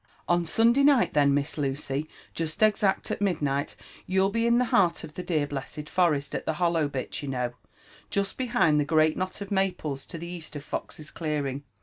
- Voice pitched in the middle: Yes, medium, 160 Hz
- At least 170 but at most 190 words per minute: No, fast, 205 wpm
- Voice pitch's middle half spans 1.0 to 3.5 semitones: No, average, 4.9 semitones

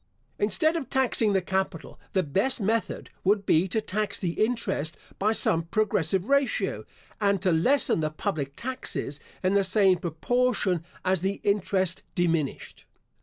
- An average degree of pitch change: Yes, average, 4.1 semitones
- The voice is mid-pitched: No, high, 195 Hz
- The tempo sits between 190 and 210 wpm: No, average, 145 wpm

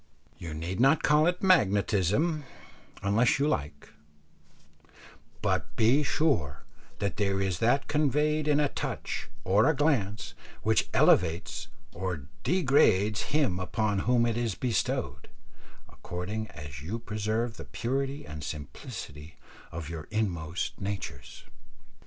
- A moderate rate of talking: No, slow, 120 wpm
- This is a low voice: Yes, low, 110 Hz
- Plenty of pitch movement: Yes, wide, 7.4 semitones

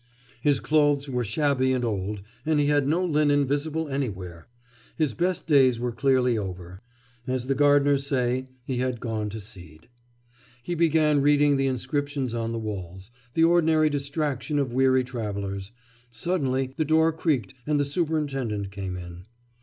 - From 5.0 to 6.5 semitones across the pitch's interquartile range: No, average, 4.6 semitones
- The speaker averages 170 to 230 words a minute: No, average, 155 wpm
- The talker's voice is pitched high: No, low, 135 Hz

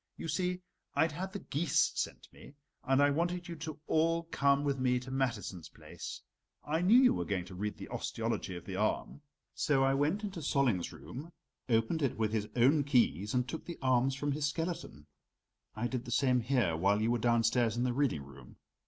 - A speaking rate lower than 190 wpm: No, fast, 205 wpm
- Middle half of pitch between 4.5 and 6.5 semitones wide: Yes, wide, 5.5 semitones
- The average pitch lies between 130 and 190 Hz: Yes, low, 135 Hz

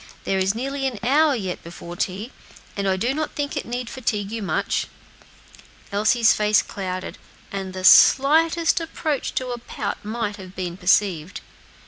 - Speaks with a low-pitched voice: No, high, 215 Hz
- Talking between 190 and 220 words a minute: No, average, 160 wpm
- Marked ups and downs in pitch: Yes, wide, 5.8 semitones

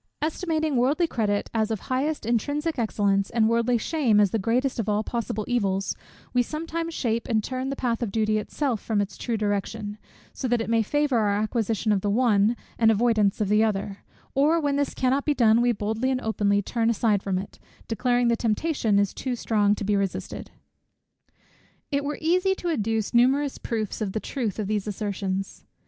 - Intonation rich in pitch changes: No, average, 3.8 semitones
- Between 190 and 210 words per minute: Yes, average, 195 wpm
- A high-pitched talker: Yes, high, 225 Hz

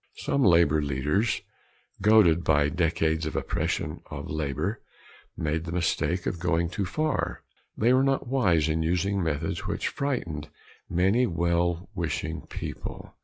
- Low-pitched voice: Yes, very low, 85 Hz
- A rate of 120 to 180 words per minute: Yes, slow, 135 wpm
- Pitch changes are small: No, average, 3.9 semitones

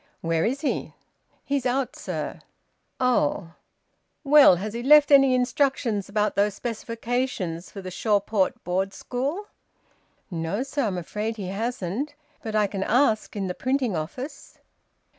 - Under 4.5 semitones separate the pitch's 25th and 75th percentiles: No, average, 5.2 semitones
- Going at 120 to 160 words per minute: Yes, average, 140 wpm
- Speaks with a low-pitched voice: No, high, 220 Hz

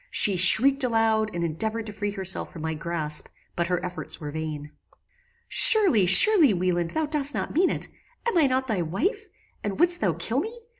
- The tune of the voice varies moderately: No, wide, 8.4 semitones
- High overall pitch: Yes, high, 210 Hz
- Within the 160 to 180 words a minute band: No, average, 190 wpm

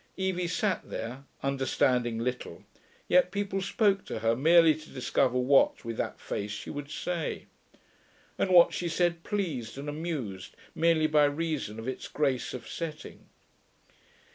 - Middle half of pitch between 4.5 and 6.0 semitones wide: Yes, wide, 5.4 semitones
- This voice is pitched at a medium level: Yes, medium, 150 Hz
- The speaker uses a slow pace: No, average, 145 wpm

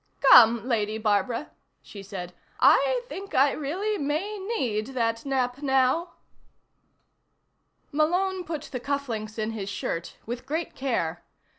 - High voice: Yes, very high, 260 Hz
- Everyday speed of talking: No, slow, 125 wpm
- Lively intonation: Yes, wide, 6.5 semitones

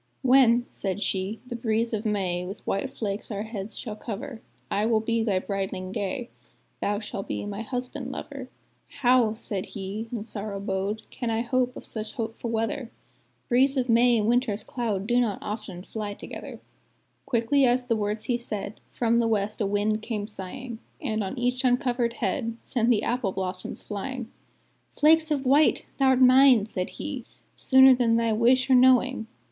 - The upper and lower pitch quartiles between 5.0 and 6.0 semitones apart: No, average, 3.3 semitones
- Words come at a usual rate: Yes, average, 175 wpm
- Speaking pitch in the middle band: No, high, 230 Hz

